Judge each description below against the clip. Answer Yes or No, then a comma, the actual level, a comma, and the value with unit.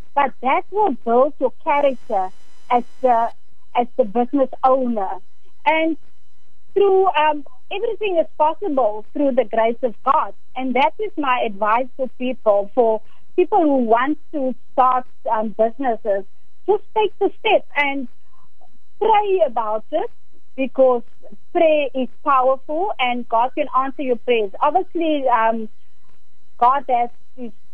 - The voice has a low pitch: No, very high, 260 Hz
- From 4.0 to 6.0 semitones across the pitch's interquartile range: Yes, average, 4.5 semitones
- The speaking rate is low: Yes, slow, 130 wpm